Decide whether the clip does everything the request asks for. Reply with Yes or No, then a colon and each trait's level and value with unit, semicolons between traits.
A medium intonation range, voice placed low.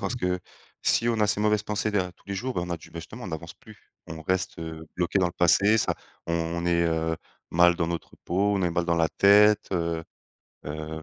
Yes: average, 3.5 semitones; very low, 90 Hz